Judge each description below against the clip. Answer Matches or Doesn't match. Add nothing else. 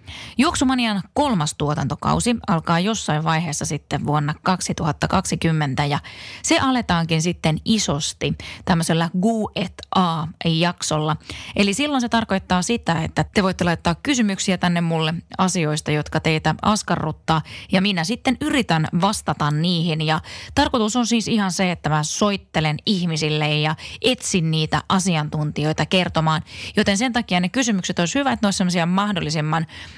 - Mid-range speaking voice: Matches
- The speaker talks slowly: Doesn't match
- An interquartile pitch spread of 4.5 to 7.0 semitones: Matches